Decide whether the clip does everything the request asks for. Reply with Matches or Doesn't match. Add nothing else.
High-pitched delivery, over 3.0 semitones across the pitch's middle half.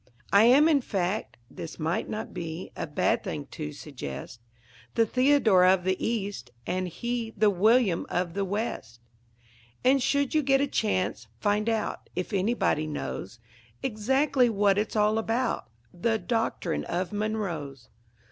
Matches